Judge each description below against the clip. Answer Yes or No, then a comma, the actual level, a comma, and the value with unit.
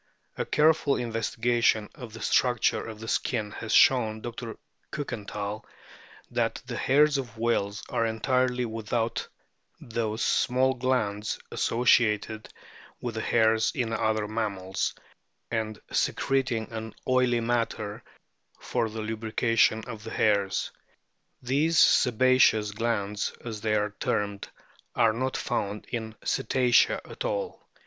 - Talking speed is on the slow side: Yes, slow, 125 wpm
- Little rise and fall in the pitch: Yes, narrow, 2.3 semitones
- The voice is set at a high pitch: No, low, 115 Hz